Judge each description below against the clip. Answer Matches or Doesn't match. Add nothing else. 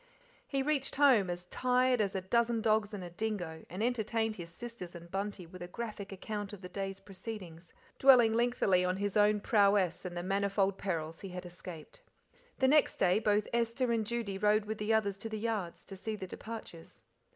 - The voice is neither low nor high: Doesn't match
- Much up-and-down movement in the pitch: Doesn't match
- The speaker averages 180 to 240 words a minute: Matches